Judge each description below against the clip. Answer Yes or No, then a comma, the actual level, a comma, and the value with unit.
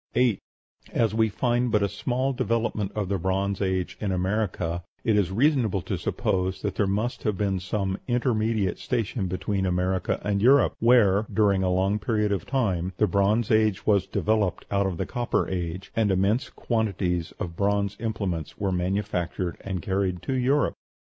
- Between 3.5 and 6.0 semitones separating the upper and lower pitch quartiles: No, average, 2.9 semitones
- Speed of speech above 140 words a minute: Yes, average, 170 wpm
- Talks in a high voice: No, low, 100 Hz